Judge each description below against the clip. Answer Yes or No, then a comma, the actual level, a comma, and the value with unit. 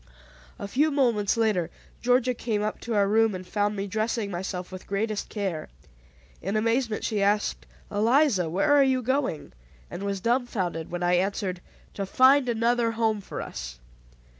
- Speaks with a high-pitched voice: Yes, high, 210 Hz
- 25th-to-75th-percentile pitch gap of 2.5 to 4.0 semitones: Yes, average, 3.7 semitones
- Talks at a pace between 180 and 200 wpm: No, average, 165 wpm